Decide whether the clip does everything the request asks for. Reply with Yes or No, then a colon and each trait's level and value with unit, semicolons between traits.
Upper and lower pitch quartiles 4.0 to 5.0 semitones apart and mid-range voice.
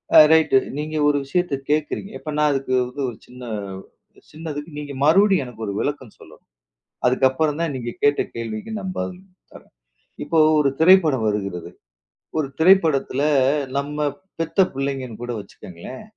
Yes: average, 4.4 semitones; medium, 145 Hz